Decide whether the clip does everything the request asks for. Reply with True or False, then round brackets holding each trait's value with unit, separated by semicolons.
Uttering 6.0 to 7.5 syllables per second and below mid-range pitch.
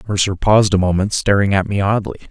True (6.4 syllables/s; 100 Hz)